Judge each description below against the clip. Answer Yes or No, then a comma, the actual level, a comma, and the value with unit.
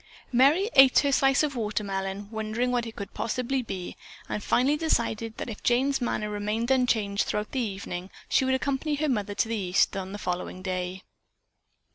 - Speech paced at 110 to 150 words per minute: No, average, 180 wpm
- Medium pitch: No, high, 225 Hz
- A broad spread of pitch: No, average, 4.6 semitones